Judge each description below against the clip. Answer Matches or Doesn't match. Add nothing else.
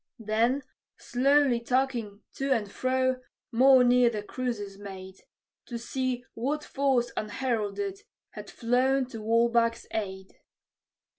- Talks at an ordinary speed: Doesn't match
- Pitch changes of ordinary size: Matches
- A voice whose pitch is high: Matches